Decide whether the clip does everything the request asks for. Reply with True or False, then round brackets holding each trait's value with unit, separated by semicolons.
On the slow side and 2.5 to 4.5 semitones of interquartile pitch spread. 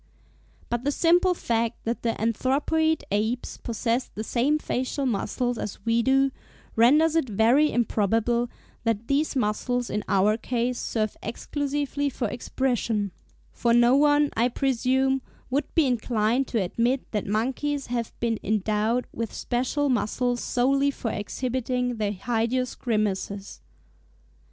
True (130 wpm; 3.1 semitones)